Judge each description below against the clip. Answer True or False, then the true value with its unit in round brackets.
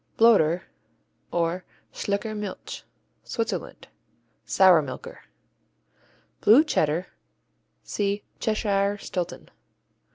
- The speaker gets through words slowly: True (70 wpm)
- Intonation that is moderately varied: True (3.6 semitones)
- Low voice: False (200 Hz)